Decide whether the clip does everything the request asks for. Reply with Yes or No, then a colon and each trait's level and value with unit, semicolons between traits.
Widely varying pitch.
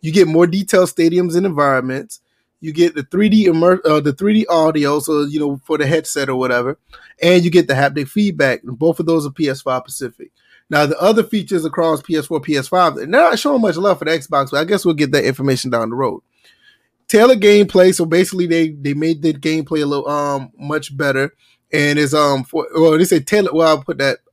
No: average, 3.8 semitones